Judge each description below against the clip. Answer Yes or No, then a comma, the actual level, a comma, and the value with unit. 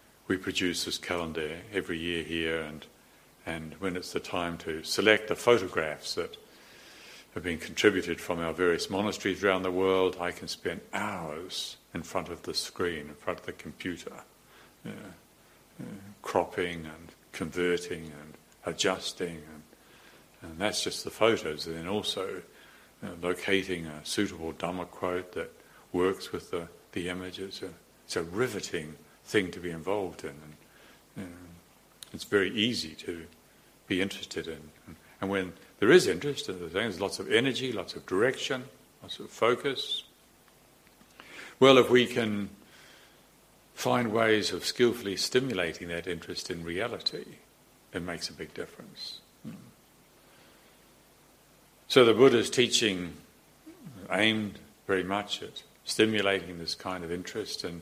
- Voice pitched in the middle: No, very low, 90 Hz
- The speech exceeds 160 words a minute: No, average, 145 wpm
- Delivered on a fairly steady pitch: No, average, 3.3 semitones